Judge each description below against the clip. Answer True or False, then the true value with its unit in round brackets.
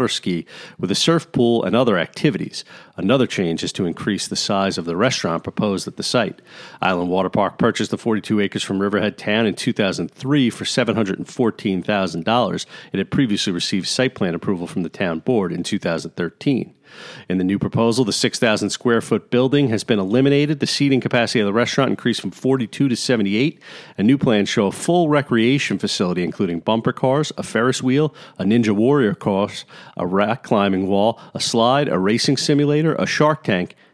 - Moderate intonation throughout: False (6.1 semitones)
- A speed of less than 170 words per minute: False (185 wpm)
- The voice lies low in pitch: True (115 Hz)